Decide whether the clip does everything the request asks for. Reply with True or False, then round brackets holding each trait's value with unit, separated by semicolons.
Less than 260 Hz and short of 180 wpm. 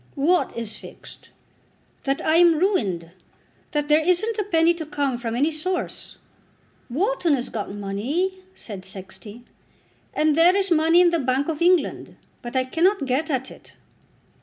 False (305 Hz; 160 wpm)